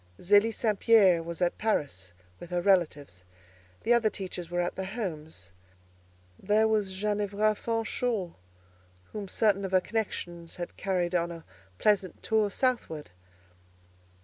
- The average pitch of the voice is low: No, high, 190 Hz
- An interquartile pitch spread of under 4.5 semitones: Yes, average, 3.7 semitones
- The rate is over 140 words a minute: No, slow, 135 wpm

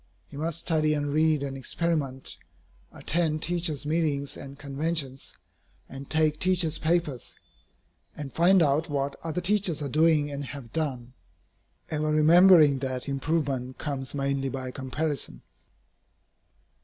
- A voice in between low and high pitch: Yes, medium, 150 Hz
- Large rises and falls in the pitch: No, average, 2.8 semitones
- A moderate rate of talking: No, slow, 125 wpm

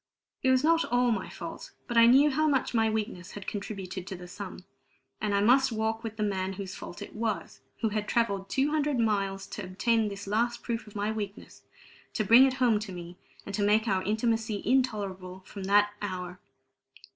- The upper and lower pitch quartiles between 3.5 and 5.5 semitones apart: No, average, 3.1 semitones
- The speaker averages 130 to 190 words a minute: No, fast, 205 wpm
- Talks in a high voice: Yes, high, 215 Hz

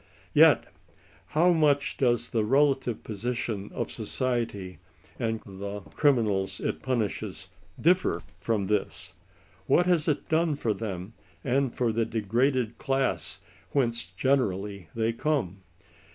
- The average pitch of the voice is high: No, low, 115 Hz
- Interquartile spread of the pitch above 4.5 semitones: Yes, average, 5.2 semitones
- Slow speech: Yes, slow, 120 wpm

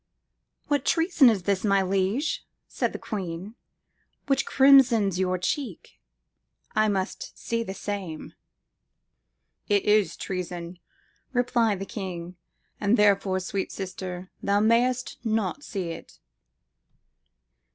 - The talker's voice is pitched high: Yes, high, 200 Hz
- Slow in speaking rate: Yes, slow, 110 wpm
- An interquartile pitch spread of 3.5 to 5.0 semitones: Yes, average, 3.9 semitones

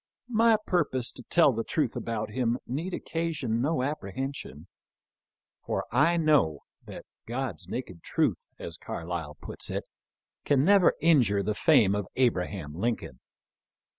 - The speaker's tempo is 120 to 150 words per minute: Yes, slow, 135 wpm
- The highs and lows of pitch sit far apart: Yes, wide, 7.2 semitones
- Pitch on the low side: Yes, low, 125 Hz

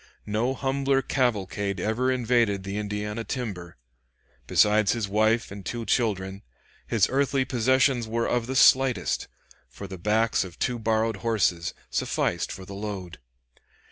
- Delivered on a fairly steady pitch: No, average, 3.7 semitones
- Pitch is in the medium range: No, low, 110 Hz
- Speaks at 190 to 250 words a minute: No, average, 140 wpm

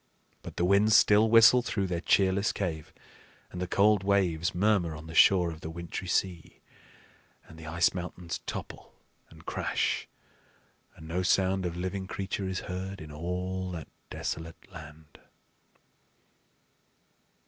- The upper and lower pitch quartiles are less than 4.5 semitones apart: Yes, average, 2.8 semitones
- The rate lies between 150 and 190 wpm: No, average, 140 wpm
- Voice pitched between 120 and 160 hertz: No, very low, 90 Hz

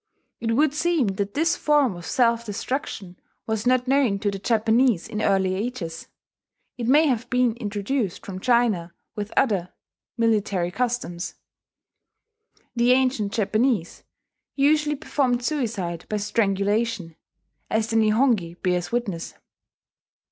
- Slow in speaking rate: Yes, slow, 125 wpm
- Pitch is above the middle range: Yes, high, 225 Hz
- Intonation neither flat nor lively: Yes, average, 4.2 semitones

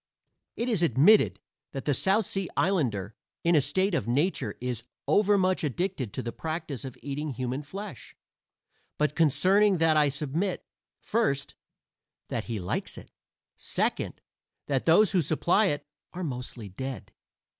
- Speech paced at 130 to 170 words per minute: Yes, average, 145 wpm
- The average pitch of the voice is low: No, medium, 150 Hz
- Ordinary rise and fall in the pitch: No, wide, 6.2 semitones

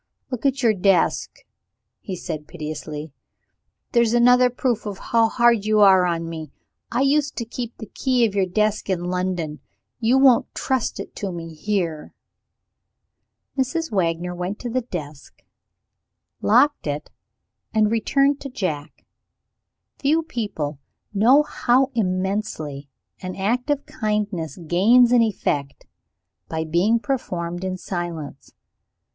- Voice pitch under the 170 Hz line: No, high, 205 Hz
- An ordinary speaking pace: No, slow, 130 wpm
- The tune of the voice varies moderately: No, wide, 6.1 semitones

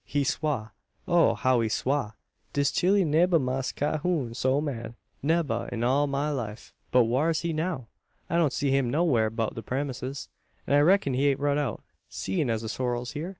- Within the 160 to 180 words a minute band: No, average, 195 wpm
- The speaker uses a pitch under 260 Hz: Yes, medium, 140 Hz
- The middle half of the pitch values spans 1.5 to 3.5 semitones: No, average, 3.9 semitones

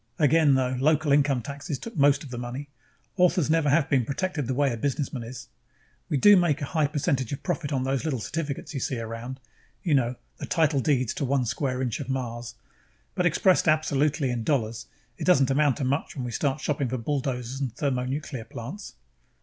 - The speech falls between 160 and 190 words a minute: No, fast, 205 wpm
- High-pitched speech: No, medium, 140 Hz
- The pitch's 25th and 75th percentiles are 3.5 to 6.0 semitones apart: No, average, 3.0 semitones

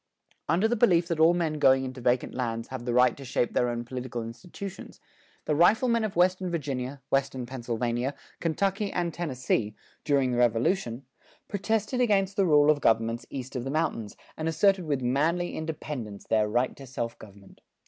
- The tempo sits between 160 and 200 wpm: Yes, average, 180 wpm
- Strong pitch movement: Yes, wide, 6.2 semitones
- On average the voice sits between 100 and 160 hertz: Yes, low, 135 Hz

